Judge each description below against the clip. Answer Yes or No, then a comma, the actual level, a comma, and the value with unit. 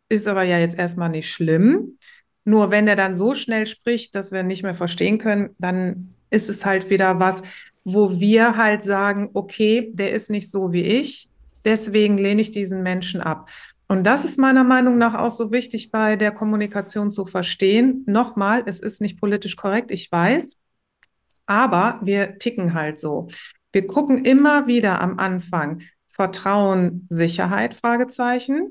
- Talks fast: No, average, 165 wpm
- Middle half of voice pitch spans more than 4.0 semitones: No, average, 3.3 semitones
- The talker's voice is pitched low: No, high, 205 Hz